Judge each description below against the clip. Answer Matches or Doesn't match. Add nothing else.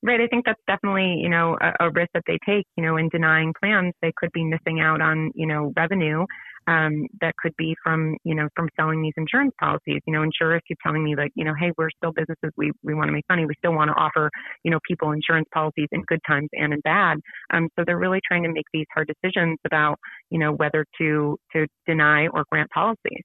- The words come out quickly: Matches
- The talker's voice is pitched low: Doesn't match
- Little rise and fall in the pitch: Matches